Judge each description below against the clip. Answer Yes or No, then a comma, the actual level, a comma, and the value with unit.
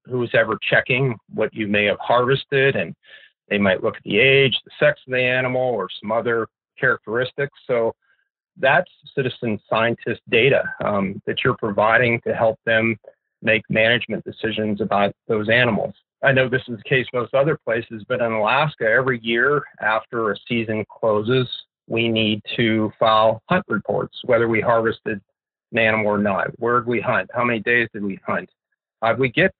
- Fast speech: No, average, 180 wpm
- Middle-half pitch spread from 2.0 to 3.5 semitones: Yes, average, 2.8 semitones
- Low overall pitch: Yes, low, 115 Hz